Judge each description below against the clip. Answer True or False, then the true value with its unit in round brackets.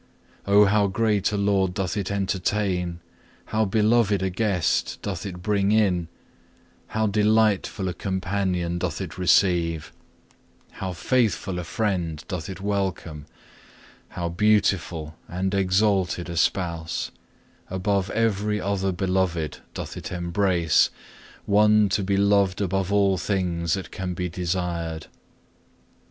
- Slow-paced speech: True (125 wpm)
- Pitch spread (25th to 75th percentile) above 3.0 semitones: False (2.5 semitones)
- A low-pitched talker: True (95 Hz)